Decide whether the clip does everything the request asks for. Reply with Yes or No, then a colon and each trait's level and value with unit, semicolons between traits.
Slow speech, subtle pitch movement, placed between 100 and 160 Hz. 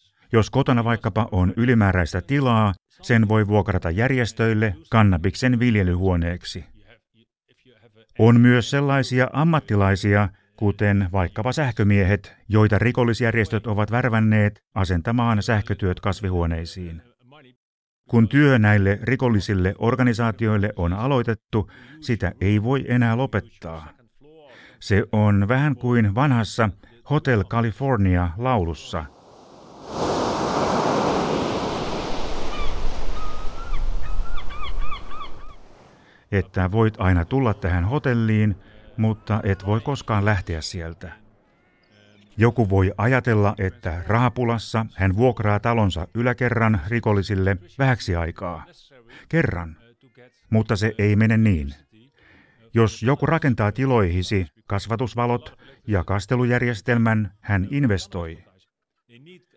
No: slow, 85 wpm; average, 3.6 semitones; low, 110 Hz